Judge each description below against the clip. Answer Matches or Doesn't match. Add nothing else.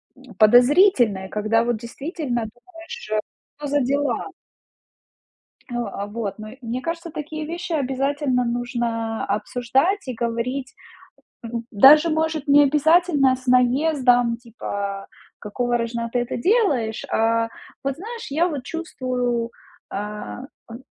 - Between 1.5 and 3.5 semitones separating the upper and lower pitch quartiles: Doesn't match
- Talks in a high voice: Matches